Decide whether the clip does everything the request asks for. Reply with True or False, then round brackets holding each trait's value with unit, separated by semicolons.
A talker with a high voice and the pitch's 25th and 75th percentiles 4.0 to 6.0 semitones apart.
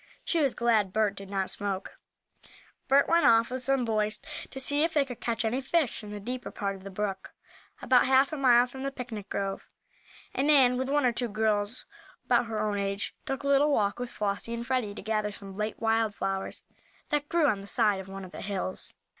True (225 Hz; 4.5 semitones)